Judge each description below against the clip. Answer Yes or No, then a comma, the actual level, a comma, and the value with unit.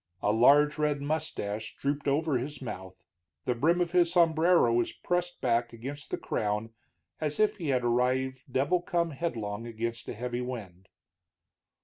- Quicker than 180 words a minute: No, average, 155 wpm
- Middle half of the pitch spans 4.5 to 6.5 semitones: Yes, average, 5.3 semitones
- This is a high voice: No, low, 130 Hz